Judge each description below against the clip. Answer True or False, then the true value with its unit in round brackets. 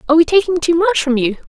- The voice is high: True (320 Hz)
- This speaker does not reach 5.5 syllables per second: False (7.4 syllables/s)